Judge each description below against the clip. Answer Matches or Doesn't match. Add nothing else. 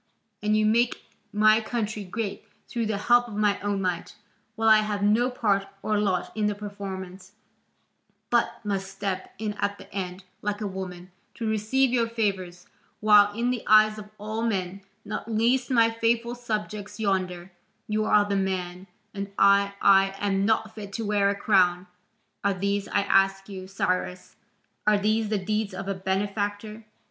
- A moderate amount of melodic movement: Doesn't match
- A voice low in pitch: Doesn't match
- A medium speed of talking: Matches